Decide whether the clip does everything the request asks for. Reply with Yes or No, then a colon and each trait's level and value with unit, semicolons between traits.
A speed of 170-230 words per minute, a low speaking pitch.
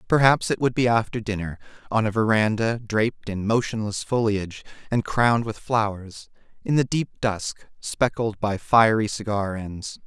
No: average, 155 wpm; low, 110 Hz